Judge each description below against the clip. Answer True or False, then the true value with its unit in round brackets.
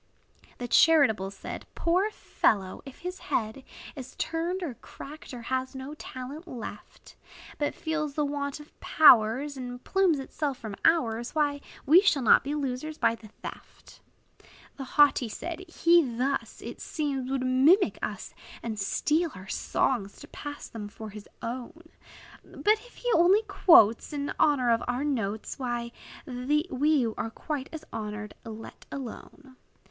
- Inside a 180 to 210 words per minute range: False (150 wpm)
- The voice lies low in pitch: False (270 Hz)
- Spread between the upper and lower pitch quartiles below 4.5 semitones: False (4.8 semitones)